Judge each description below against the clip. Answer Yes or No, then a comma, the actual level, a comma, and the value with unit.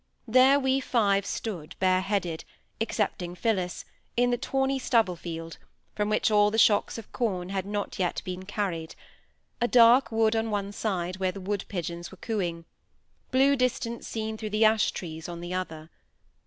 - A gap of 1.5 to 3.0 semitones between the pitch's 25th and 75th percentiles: No, average, 3.9 semitones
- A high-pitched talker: Yes, high, 205 Hz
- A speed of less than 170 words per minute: Yes, average, 160 wpm